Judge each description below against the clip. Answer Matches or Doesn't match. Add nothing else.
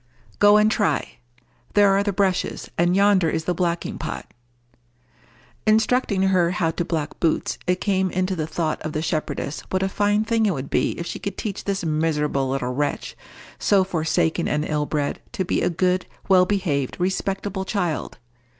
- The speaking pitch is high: Doesn't match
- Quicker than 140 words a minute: Matches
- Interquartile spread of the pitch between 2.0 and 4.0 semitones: Matches